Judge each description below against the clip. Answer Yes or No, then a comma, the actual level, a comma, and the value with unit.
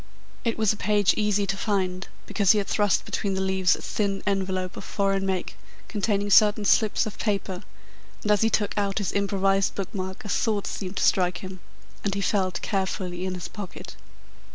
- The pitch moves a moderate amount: No, narrow, 1.6 semitones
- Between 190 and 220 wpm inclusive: Yes, average, 195 wpm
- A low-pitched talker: No, high, 195 Hz